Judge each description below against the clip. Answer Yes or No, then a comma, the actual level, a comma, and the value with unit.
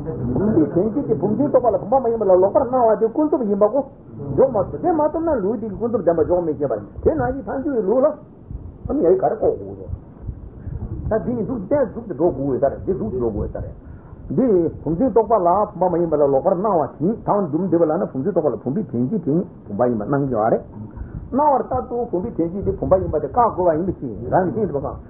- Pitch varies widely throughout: Yes, wide, 7.3 semitones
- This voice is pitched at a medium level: No, high, 205 Hz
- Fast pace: Yes, fast, 175 wpm